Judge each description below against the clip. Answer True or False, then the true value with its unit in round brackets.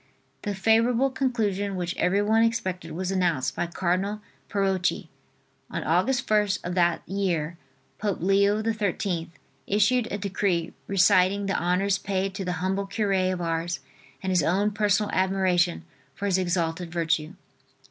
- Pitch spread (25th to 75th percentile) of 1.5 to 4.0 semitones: True (2.5 semitones)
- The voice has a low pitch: False (190 Hz)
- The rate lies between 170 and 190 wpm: False (140 wpm)